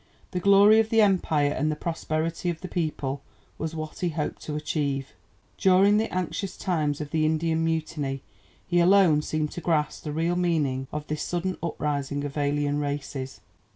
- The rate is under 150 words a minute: No, average, 175 wpm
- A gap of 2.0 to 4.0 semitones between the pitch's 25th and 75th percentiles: Yes, average, 3.1 semitones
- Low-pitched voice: No, medium, 155 Hz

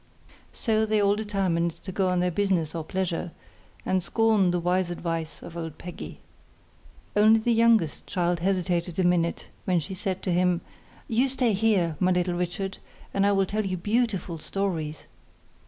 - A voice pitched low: No, medium, 185 Hz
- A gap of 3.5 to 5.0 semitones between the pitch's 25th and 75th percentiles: No, average, 2.9 semitones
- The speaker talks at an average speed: Yes, average, 170 wpm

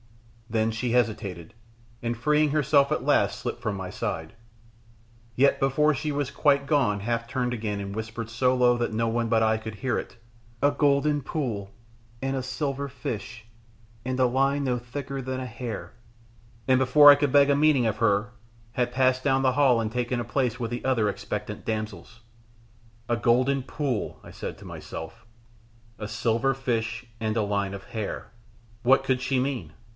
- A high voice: No, low, 125 Hz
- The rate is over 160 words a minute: Yes, average, 180 wpm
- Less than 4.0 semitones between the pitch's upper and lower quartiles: Yes, average, 3.4 semitones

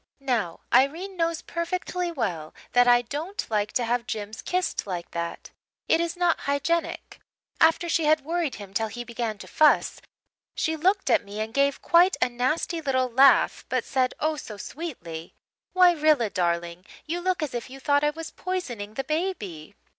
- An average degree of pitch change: No, wide, 7.2 semitones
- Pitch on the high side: Yes, very high, 275 Hz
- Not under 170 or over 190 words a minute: Yes, average, 180 wpm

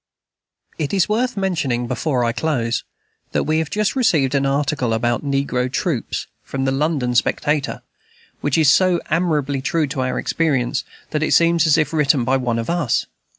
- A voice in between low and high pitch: Yes, medium, 145 Hz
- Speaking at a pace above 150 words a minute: Yes, average, 175 wpm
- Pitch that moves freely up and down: No, average, 4.2 semitones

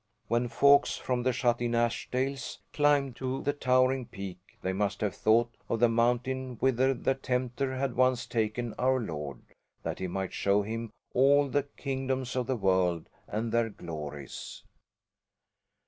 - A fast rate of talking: No, average, 155 wpm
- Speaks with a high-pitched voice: No, low, 120 Hz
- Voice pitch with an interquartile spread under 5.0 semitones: Yes, average, 3.7 semitones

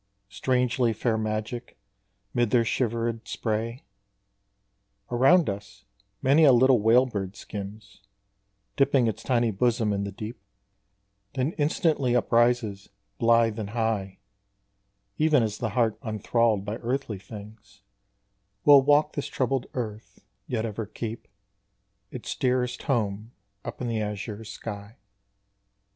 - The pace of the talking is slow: Yes, slow, 120 wpm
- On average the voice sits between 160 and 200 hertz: No, low, 115 Hz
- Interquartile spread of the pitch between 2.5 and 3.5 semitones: Yes, average, 2.9 semitones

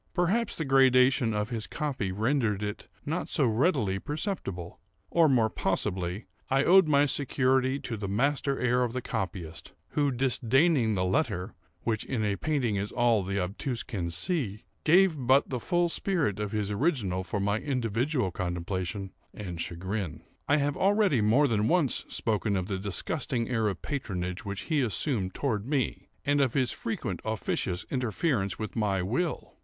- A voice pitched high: No, low, 115 Hz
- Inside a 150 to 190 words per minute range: Yes, average, 165 wpm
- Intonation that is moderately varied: No, wide, 6.1 semitones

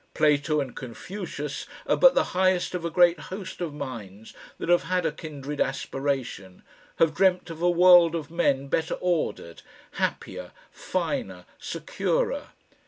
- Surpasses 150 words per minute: No, average, 145 wpm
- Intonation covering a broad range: No, average, 4.4 semitones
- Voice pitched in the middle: Yes, medium, 155 Hz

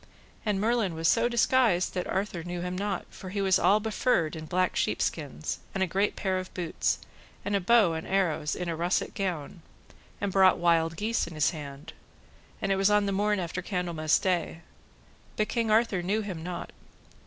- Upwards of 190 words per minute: Yes, average, 200 wpm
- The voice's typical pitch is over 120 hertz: Yes, medium, 185 Hz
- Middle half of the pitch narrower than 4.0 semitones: Yes, average, 3.5 semitones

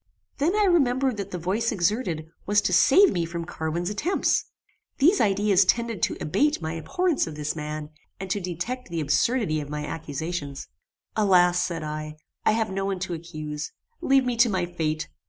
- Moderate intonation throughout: No, wide, 6.4 semitones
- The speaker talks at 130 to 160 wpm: No, average, 180 wpm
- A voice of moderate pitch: Yes, medium, 180 Hz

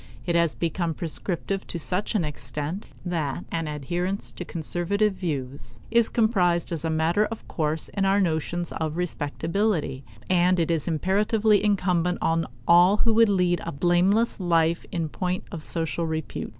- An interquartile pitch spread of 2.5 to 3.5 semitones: Yes, average, 3.2 semitones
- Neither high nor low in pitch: Yes, medium, 175 Hz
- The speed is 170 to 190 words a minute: No, average, 160 wpm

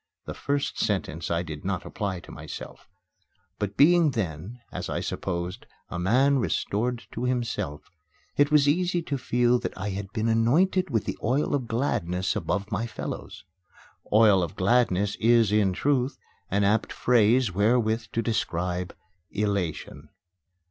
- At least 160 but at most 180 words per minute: No, average, 150 wpm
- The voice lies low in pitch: Yes, low, 110 Hz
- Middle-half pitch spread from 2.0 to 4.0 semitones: No, average, 4.8 semitones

